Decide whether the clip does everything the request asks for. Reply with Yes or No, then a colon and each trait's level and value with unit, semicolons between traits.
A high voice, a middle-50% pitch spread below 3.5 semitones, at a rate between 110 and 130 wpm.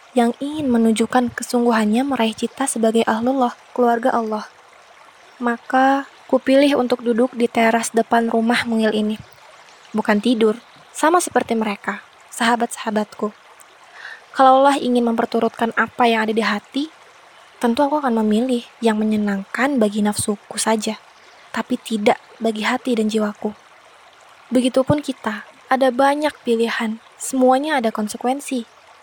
Yes: high, 235 Hz; narrow, 2.5 semitones; average, 120 wpm